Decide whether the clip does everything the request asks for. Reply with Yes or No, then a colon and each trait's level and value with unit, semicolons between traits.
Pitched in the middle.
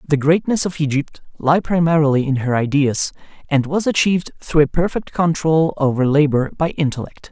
Yes: medium, 155 Hz